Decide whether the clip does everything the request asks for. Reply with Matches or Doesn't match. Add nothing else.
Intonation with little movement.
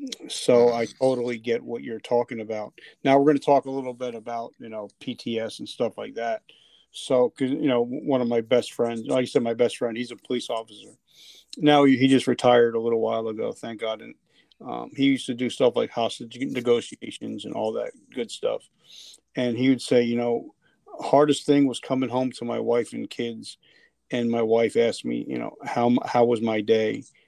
Matches